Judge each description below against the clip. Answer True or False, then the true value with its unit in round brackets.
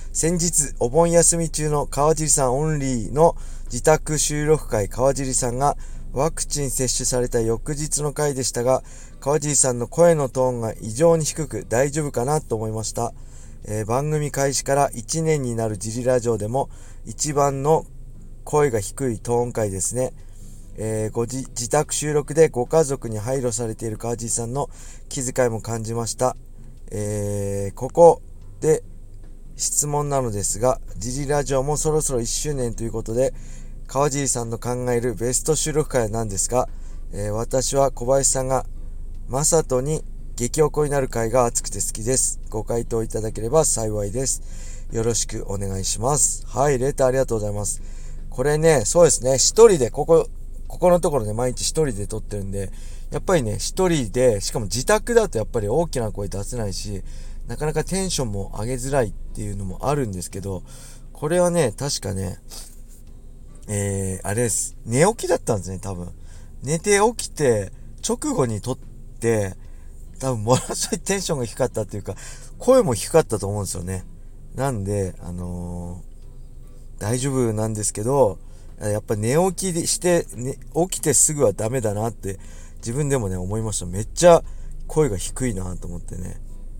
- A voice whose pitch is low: True (120 Hz)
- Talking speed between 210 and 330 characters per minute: True (325 characters per minute)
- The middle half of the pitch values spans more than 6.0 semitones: False (5.4 semitones)